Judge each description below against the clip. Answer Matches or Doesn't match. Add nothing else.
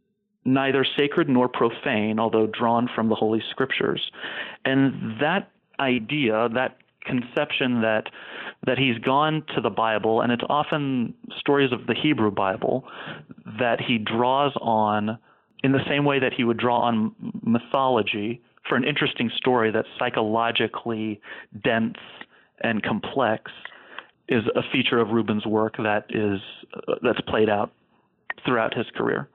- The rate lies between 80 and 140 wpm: Matches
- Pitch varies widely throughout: Doesn't match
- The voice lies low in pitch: Matches